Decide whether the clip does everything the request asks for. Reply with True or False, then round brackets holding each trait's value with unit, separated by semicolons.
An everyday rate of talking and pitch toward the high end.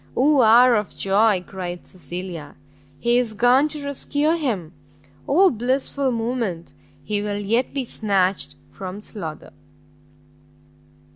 False (120 wpm; 220 Hz)